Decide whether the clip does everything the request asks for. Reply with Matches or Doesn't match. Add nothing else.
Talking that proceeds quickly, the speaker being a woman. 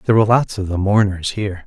Doesn't match